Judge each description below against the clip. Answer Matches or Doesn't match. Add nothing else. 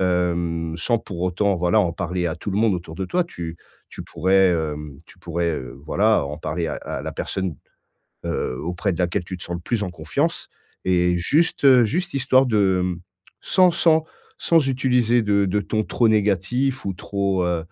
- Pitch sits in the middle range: Doesn't match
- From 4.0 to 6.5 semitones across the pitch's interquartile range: Matches